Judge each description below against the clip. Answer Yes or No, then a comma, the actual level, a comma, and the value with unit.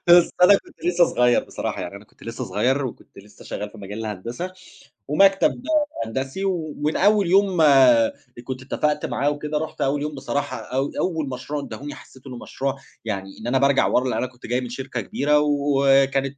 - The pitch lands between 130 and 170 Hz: Yes, low, 135 Hz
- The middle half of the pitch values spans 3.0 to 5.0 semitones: Yes, average, 3.5 semitones